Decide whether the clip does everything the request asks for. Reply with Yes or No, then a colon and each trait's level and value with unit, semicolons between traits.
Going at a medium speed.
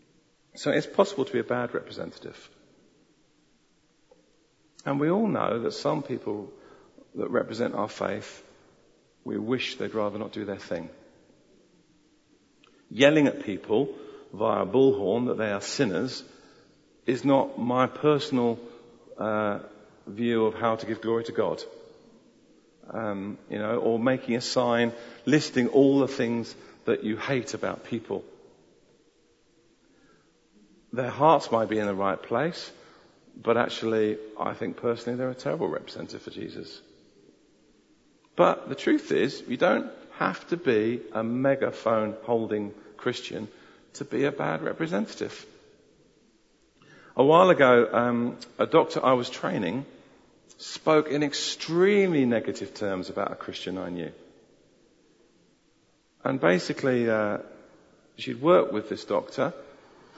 No: slow, 130 wpm